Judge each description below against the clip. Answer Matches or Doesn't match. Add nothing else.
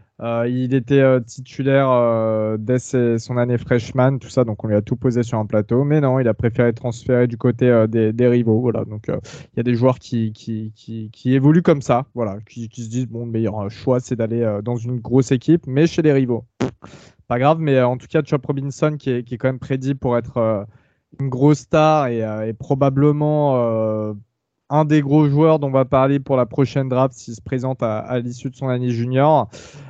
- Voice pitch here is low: Matches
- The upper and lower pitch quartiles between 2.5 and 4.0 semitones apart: Matches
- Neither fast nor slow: Doesn't match